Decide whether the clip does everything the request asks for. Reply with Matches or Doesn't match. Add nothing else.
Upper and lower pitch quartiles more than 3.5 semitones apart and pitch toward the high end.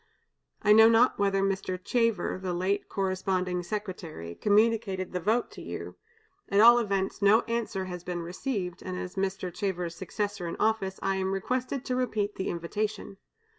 Doesn't match